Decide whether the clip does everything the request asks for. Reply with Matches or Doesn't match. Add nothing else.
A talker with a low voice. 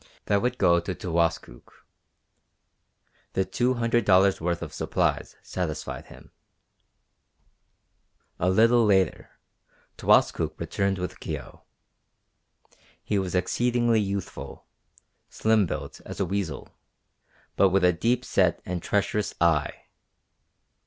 Matches